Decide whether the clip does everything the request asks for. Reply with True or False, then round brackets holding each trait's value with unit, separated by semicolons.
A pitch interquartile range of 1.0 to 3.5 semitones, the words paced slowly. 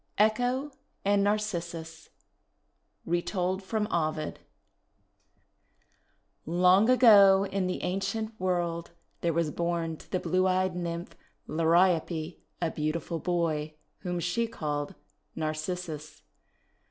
True (2.8 semitones; 100 wpm)